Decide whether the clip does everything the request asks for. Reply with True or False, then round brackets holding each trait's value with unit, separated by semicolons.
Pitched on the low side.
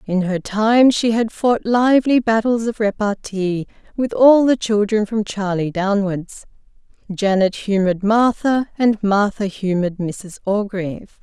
False (210 Hz)